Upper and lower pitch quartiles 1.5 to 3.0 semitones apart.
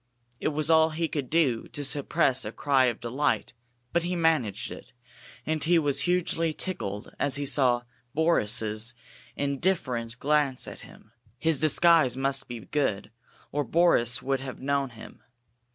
No: average, 4.3 semitones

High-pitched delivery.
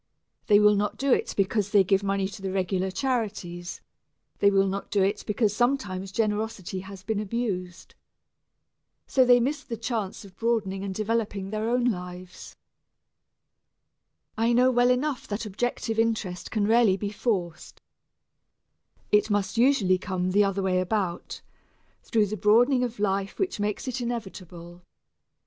Yes: high, 205 Hz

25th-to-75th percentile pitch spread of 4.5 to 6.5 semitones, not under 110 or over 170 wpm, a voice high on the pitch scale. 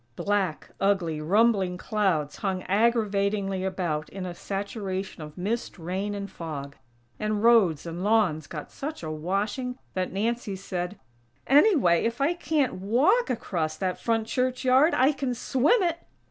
Yes: average, 4.8 semitones; average, 145 wpm; high, 200 Hz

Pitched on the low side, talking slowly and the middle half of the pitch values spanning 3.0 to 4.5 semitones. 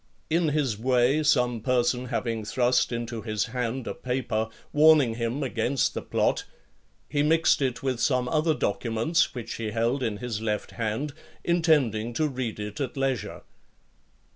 No: low, 125 Hz; average, 155 wpm; average, 3.5 semitones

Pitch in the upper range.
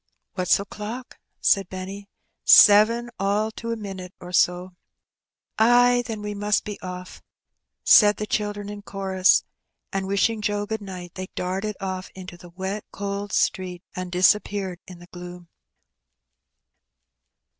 Yes: high, 200 Hz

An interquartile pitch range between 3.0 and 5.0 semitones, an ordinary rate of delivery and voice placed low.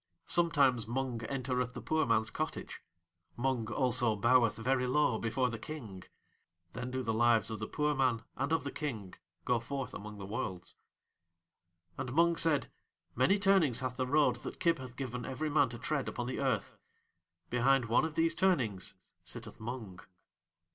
Yes: average, 3.8 semitones; average, 170 wpm; low, 125 Hz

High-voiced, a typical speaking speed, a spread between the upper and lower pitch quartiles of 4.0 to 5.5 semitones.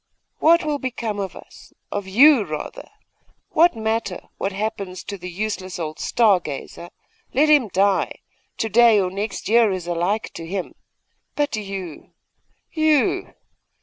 Yes: high, 205 Hz; average, 145 wpm; average, 4.3 semitones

